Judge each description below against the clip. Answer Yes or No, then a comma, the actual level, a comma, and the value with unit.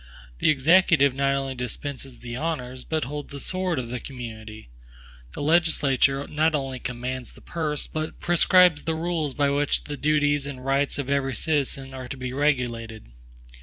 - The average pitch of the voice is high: No, medium, 140 Hz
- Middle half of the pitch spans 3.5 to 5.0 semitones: No, average, 3.0 semitones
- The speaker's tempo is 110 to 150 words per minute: No, average, 165 wpm